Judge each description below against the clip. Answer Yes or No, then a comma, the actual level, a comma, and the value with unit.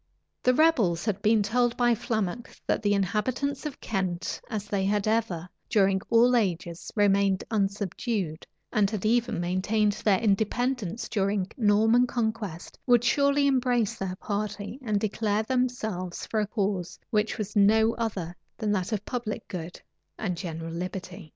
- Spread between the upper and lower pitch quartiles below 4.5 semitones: Yes, average, 3.3 semitones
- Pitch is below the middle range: No, high, 210 Hz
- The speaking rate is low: No, average, 150 wpm